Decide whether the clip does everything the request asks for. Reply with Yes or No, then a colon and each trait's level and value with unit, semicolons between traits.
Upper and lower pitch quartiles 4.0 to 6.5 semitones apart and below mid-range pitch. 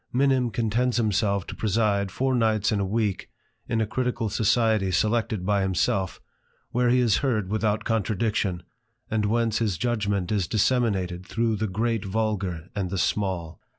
No: average, 2.9 semitones; low, 110 Hz